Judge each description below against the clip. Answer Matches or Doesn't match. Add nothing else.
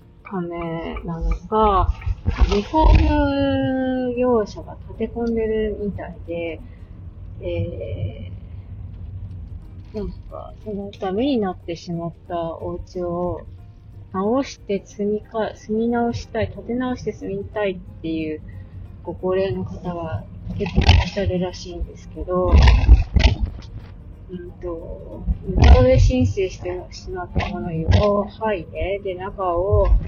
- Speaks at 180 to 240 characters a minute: Matches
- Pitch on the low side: Matches